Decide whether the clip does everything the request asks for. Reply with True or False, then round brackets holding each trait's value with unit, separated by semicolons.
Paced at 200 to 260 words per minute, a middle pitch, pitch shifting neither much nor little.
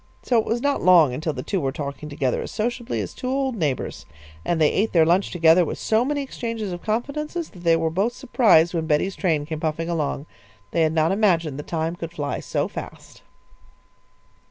False (205 wpm; 170 Hz; 6.0 semitones)